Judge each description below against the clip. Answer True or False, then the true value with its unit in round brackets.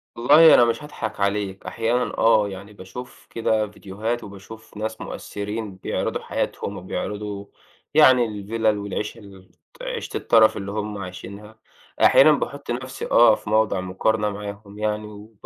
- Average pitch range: False (2.1 semitones)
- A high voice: False (105 Hz)